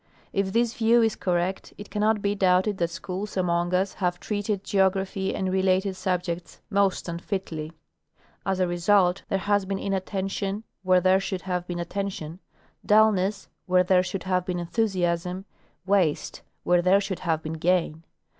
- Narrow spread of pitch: Yes, narrow, 1.9 semitones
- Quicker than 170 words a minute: No, average, 160 wpm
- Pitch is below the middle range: No, high, 190 Hz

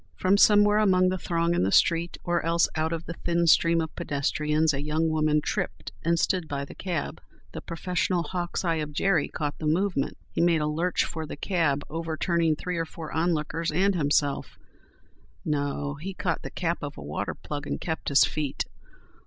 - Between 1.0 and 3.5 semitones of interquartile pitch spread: Yes, narrow, 2.4 semitones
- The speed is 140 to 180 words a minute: No, average, 190 wpm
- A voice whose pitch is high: No, medium, 165 Hz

